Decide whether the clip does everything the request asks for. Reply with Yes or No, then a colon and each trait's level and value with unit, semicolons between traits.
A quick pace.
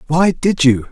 No: average, 195 wpm